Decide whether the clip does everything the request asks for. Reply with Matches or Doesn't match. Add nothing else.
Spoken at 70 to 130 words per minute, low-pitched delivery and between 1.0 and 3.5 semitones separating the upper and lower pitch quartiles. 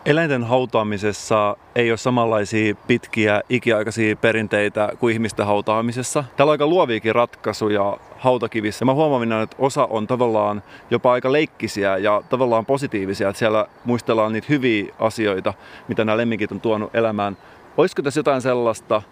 Doesn't match